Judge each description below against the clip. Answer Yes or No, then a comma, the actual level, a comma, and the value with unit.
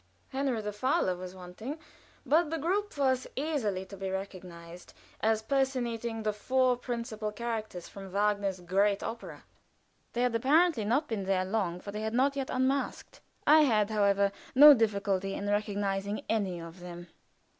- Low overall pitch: No, high, 215 Hz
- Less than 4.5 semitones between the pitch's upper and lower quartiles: No, average, 4.8 semitones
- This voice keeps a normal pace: Yes, average, 155 wpm